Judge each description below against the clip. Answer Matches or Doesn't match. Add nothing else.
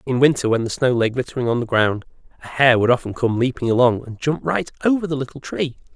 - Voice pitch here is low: Matches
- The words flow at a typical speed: Doesn't match